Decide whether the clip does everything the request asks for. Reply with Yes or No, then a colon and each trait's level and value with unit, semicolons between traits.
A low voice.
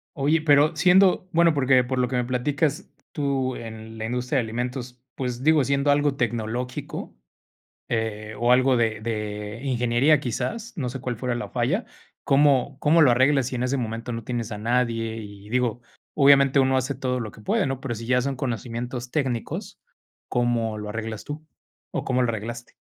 Yes: low, 125 Hz